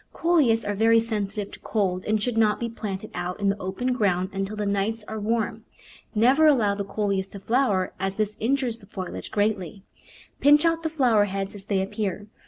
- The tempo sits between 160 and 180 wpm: No, average, 200 wpm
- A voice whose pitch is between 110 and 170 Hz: No, high, 210 Hz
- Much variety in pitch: No, average, 2.8 semitones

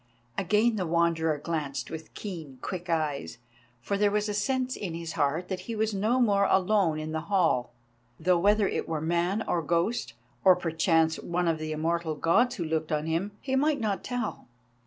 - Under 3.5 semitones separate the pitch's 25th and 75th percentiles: No, average, 4.3 semitones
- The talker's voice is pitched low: No, medium, 175 Hz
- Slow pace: No, average, 190 wpm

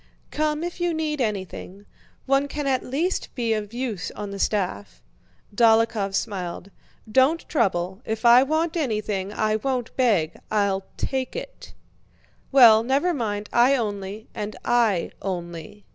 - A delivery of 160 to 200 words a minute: No, slow, 135 wpm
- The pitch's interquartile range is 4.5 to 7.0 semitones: Yes, average, 5.1 semitones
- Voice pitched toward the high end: Yes, high, 220 Hz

